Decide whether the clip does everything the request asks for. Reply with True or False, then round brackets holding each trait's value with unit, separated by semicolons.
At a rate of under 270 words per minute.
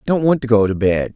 False (310 wpm)